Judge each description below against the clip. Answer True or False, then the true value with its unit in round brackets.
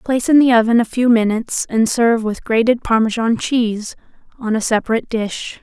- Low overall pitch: False (230 Hz)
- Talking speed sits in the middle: True (180 wpm)